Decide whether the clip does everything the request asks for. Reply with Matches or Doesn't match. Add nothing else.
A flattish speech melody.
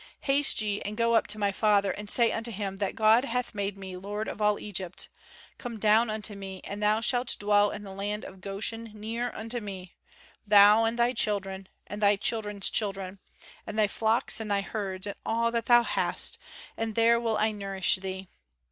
Matches